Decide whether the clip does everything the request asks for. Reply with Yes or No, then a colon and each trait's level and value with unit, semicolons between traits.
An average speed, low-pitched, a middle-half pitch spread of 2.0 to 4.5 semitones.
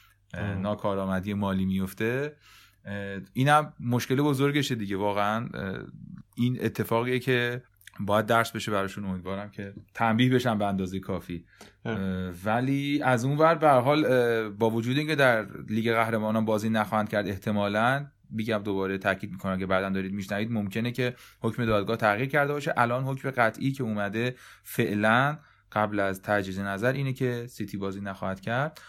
Yes: average, 145 wpm; low, 110 Hz; average, 3.9 semitones